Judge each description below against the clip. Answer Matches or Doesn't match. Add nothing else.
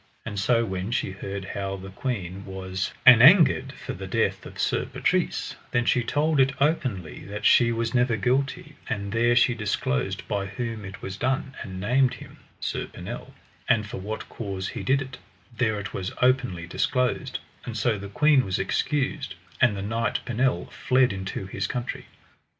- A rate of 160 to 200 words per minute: Matches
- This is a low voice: Matches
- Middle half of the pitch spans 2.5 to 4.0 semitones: Doesn't match